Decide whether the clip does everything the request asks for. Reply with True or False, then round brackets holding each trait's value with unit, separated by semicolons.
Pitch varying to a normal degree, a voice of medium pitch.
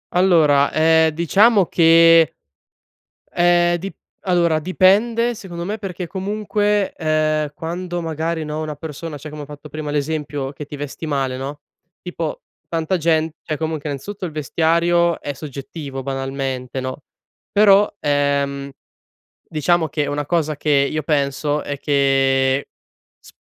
True (3.2 semitones; 155 Hz)